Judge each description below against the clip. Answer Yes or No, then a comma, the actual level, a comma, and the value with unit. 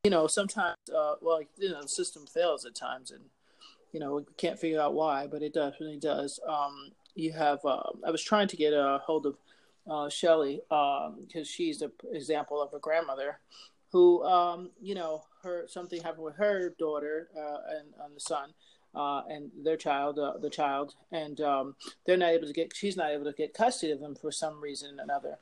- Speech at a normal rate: No, fast, 210 wpm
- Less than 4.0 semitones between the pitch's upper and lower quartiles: Yes, average, 2.9 semitones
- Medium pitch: Yes, medium, 155 Hz